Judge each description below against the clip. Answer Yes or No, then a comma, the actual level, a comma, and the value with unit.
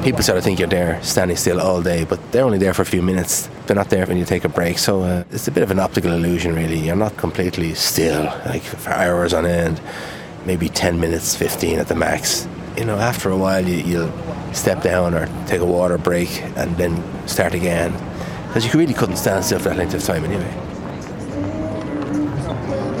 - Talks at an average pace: No, fast, 215 wpm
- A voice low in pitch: Yes, very low, 90 Hz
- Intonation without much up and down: Yes, narrow, 2.2 semitones